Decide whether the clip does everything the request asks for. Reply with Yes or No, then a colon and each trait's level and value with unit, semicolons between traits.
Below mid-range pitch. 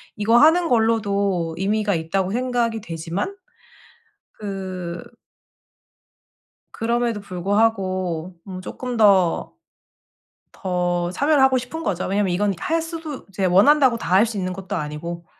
No: high, 200 Hz